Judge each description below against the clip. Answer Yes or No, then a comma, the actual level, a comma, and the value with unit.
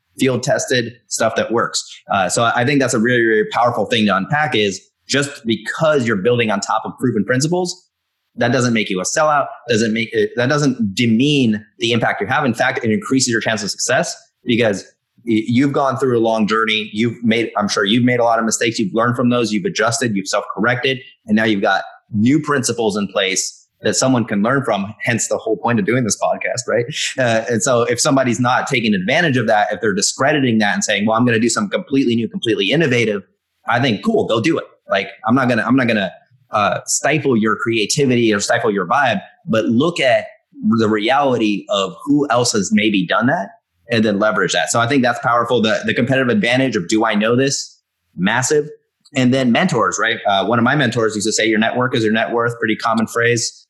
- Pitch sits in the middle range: No, low, 120 Hz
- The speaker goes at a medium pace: No, fast, 220 wpm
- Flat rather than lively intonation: No, average, 3.4 semitones